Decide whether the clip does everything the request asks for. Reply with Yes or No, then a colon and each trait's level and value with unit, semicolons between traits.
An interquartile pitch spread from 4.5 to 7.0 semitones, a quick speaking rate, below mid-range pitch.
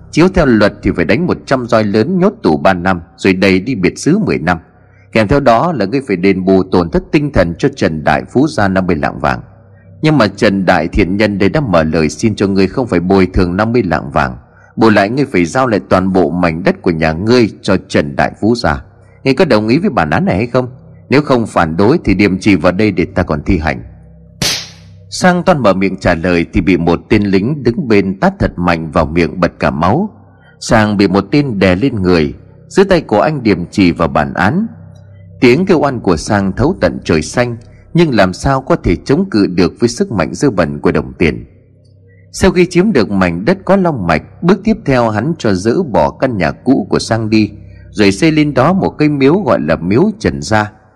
No: average, 5.2 semitones; average, 235 wpm; low, 100 Hz